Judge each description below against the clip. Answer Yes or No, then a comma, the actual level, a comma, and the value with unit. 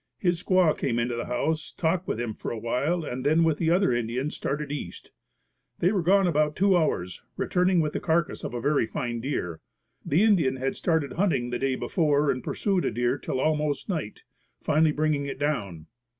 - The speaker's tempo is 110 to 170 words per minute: No, average, 200 wpm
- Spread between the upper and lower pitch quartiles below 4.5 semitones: No, average, 5.2 semitones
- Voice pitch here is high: No, medium, 150 Hz